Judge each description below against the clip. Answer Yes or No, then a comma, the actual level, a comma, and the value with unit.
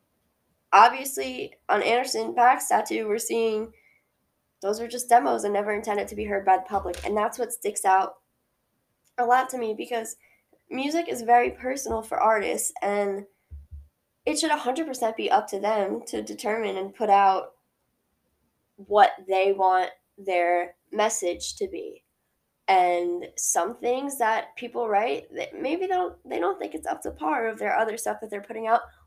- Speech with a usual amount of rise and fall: Yes, average, 3.9 semitones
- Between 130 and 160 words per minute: No, average, 170 wpm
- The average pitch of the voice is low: No, high, 210 Hz